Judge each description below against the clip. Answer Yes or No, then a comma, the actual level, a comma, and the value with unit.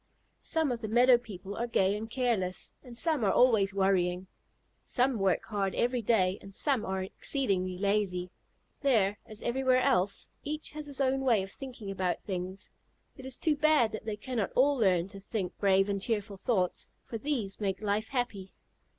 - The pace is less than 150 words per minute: No, average, 180 wpm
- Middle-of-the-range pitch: No, high, 215 Hz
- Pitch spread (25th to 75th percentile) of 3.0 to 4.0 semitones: No, average, 4.7 semitones